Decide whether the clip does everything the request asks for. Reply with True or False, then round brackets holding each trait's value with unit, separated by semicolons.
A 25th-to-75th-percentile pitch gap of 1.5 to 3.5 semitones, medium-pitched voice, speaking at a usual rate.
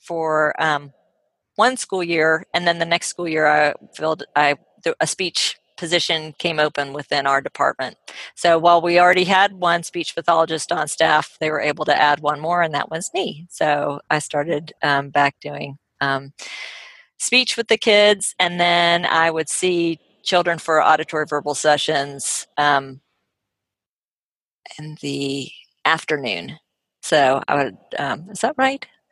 True (3.0 semitones; 160 Hz; 155 wpm)